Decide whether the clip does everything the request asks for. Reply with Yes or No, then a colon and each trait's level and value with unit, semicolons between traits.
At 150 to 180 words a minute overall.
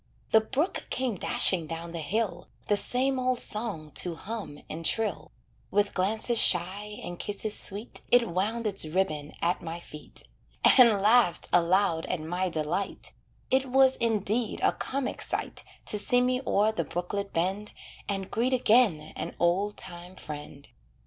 Yes: average, 155 wpm